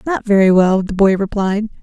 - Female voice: Yes, female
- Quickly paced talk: No, average, 195 wpm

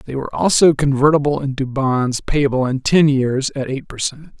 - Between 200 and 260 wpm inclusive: Yes, fast, 205 wpm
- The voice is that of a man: Yes, male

